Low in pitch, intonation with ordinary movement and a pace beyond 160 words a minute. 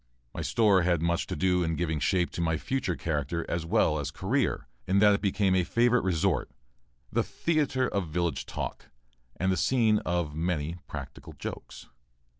Yes: very low, 90 Hz; average, 4.0 semitones; average, 175 wpm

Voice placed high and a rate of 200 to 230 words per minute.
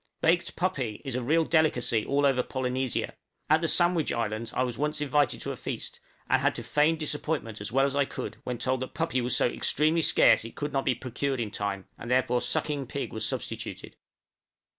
No: low, 130 Hz; fast, 205 wpm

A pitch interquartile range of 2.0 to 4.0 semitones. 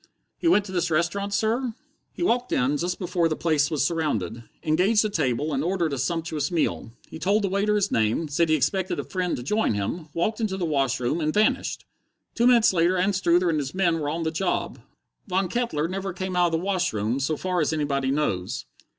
No: average, 4.5 semitones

